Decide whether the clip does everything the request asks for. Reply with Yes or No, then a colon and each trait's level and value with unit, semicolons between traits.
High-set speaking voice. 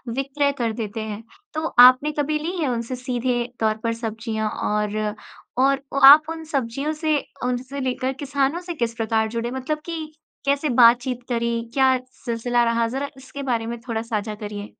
Yes: high, 245 Hz